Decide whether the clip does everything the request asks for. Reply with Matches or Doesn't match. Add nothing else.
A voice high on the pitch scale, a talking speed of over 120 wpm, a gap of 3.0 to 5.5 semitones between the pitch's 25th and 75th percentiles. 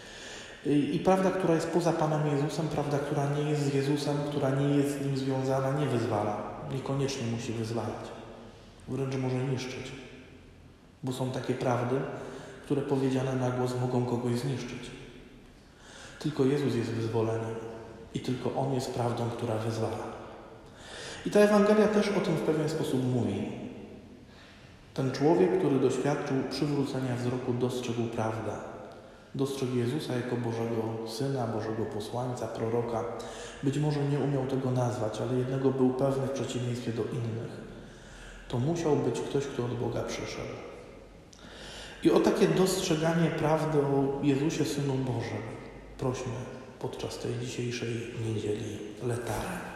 Doesn't match